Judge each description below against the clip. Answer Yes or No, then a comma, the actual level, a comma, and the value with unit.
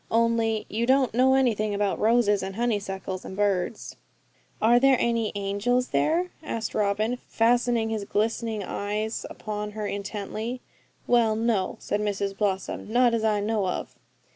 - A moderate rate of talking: Yes, average, 145 wpm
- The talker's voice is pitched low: No, high, 220 Hz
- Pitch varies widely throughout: No, narrow, 2.5 semitones